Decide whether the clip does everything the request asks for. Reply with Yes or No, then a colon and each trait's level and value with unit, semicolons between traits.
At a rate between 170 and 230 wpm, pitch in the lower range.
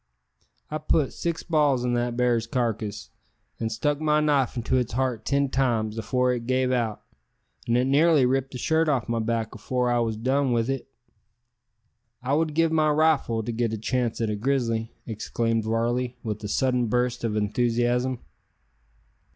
Yes: average, 175 wpm; low, 125 Hz